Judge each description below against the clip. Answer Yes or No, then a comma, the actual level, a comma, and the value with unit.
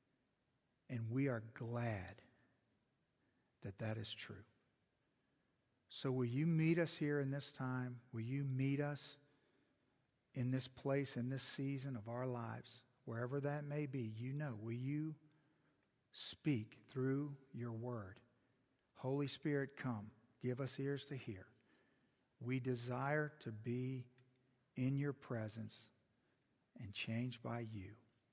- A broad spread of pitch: No, average, 3.0 semitones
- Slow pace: Yes, slow, 130 wpm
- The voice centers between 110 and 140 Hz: Yes, low, 125 Hz